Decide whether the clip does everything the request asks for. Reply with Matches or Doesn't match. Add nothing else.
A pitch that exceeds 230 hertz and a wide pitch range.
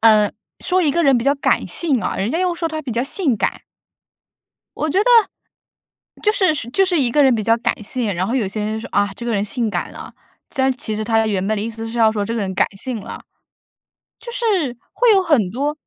Matches